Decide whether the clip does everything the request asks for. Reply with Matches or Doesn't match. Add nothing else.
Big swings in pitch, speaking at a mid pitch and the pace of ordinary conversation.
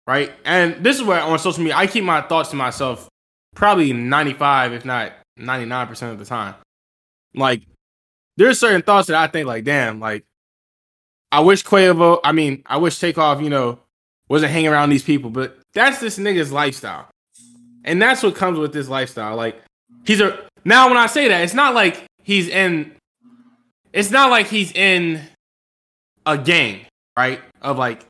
Matches